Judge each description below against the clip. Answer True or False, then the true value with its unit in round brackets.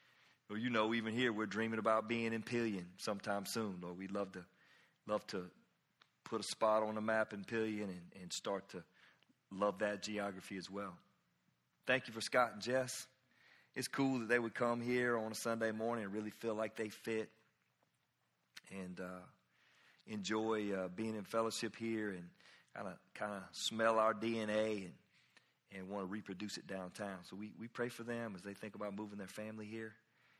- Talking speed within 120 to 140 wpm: False (185 wpm)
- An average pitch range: False (2.1 semitones)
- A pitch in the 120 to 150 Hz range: False (110 Hz)